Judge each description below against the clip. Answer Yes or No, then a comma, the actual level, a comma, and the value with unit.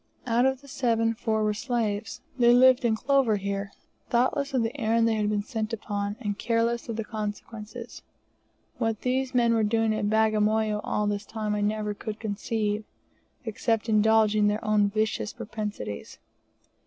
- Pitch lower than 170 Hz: No, high, 220 Hz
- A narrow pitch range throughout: Yes, narrow, 1.7 semitones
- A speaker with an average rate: Yes, average, 165 wpm